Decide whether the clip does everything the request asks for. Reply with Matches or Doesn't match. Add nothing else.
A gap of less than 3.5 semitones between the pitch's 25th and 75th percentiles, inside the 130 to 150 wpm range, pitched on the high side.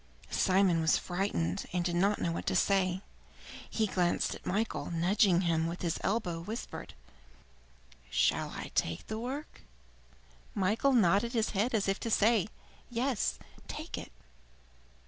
Doesn't match